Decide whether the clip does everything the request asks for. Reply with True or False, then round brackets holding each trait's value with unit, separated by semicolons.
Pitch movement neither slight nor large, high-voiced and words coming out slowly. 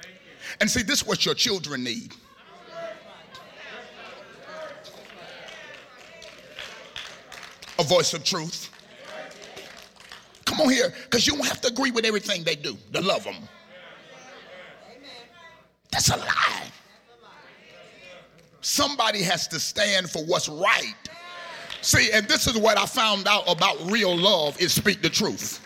False (7.3 semitones; 205 Hz; 125 wpm)